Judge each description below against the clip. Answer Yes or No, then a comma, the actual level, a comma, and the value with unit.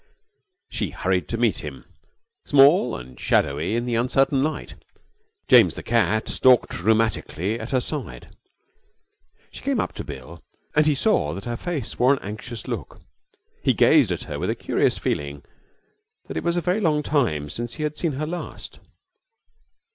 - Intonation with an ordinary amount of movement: No, wide, 8.0 semitones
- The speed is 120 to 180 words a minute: Yes, average, 170 wpm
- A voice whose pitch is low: Yes, low, 120 Hz